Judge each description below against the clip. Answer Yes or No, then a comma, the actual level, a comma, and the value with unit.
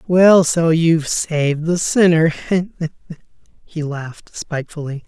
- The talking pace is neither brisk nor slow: No, slow, 105 wpm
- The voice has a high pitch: No, medium, 160 Hz